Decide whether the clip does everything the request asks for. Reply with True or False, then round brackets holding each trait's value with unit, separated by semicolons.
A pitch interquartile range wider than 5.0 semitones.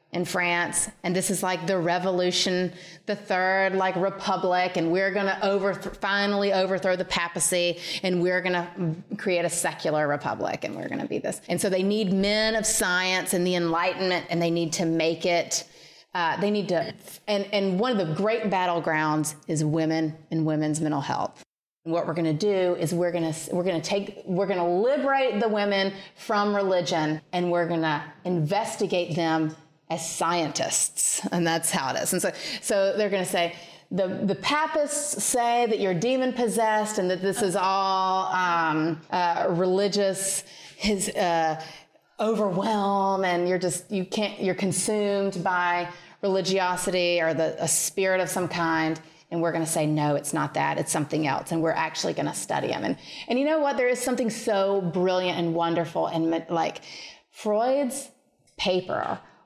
False (3.0 semitones)